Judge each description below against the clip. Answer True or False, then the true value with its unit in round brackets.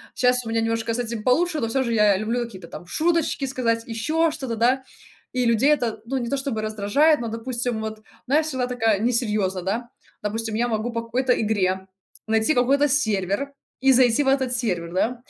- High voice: True (235 Hz)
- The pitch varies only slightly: False (3.0 semitones)